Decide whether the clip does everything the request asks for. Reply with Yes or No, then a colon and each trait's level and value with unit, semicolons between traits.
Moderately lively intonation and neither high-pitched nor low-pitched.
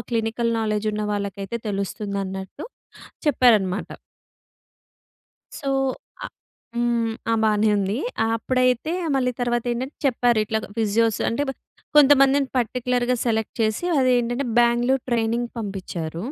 No: average, 3.0 semitones; high, 230 Hz